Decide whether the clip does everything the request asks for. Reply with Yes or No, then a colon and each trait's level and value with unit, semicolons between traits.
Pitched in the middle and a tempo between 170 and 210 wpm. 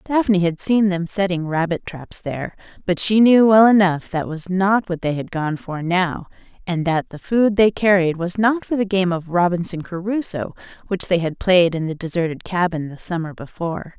Yes: medium, 180 Hz; average, 200 wpm